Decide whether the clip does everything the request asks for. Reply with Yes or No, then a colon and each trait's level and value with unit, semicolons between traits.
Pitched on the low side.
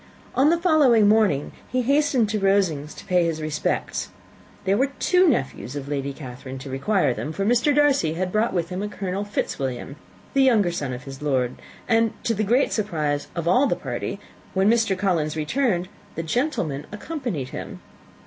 No: high, 190 Hz